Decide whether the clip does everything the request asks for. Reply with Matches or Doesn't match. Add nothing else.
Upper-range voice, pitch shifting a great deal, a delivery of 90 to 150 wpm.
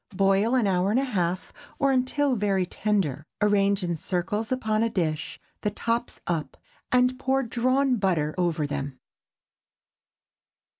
Matches